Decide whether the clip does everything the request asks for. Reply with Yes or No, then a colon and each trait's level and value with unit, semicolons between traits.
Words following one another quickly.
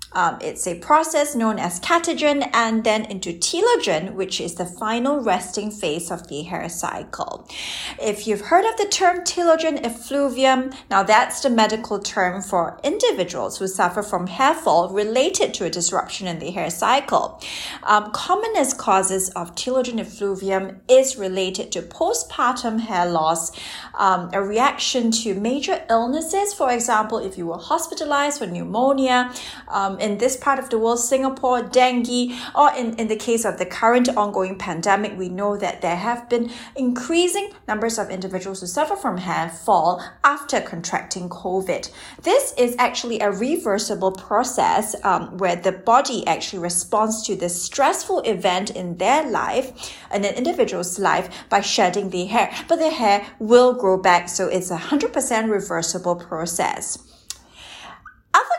No: average, 155 wpm